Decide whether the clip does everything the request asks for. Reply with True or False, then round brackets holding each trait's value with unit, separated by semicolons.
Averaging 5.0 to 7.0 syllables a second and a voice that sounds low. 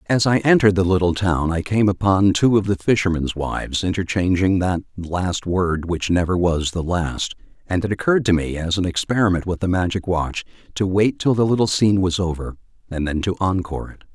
True (5.5 syllables/s; 95 Hz)